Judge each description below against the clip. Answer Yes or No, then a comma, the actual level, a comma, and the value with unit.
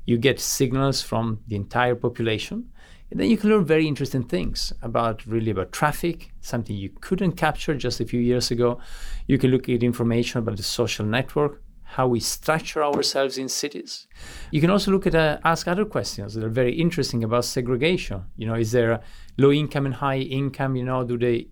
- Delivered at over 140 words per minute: Yes, average, 200 wpm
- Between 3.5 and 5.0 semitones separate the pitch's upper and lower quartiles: Yes, average, 4.2 semitones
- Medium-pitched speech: No, low, 130 Hz